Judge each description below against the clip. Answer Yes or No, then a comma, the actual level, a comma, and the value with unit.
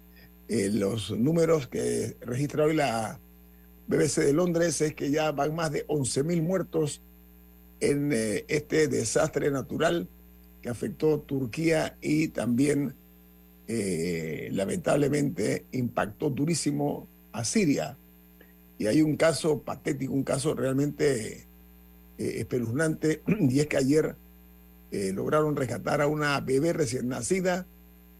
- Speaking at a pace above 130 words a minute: No, slow, 125 wpm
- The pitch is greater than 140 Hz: No, low, 135 Hz